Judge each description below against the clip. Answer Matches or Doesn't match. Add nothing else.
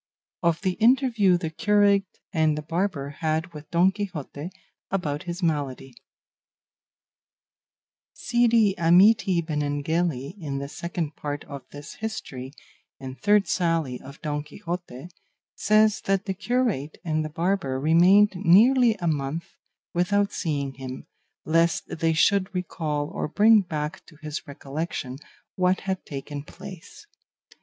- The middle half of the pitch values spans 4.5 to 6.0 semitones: Matches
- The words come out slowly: Matches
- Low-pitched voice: Doesn't match